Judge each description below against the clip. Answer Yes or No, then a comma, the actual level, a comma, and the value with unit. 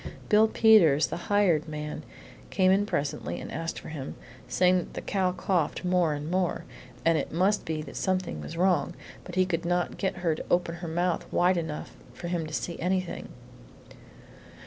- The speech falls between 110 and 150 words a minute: No, average, 185 wpm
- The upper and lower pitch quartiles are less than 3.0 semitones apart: Yes, narrow, 2.5 semitones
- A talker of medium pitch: Yes, medium, 175 Hz